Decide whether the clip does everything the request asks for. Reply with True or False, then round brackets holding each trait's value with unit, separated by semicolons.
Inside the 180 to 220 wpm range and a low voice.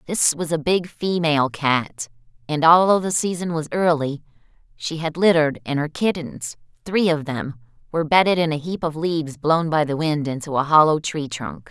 False (190 wpm; 155 Hz)